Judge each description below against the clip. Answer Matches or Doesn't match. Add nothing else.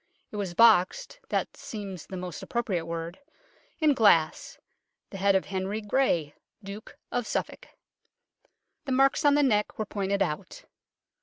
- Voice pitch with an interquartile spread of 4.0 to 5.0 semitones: Matches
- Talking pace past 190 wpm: Doesn't match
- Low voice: Doesn't match